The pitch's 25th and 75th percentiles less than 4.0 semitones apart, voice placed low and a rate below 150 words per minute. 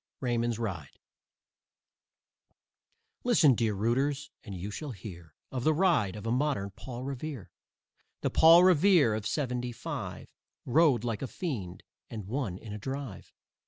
No: wide, 5.5 semitones; low, 120 Hz; average, 140 wpm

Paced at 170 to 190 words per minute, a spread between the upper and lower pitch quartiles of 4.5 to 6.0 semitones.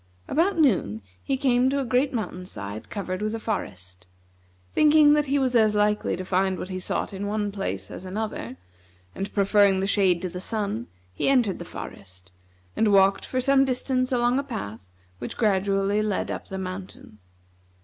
Yes: average, 180 wpm; average, 5.2 semitones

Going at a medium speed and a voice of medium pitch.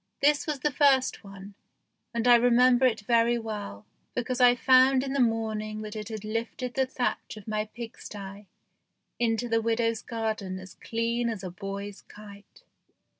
No: average, 165 wpm; high, 225 Hz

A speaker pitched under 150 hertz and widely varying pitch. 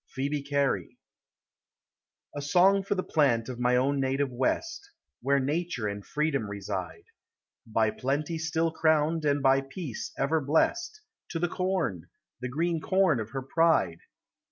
No: medium, 140 Hz; average, 4.7 semitones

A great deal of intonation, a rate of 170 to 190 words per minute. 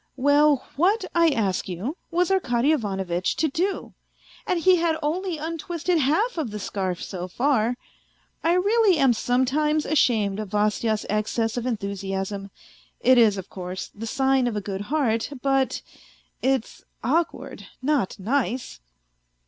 No: wide, 7.0 semitones; average, 145 wpm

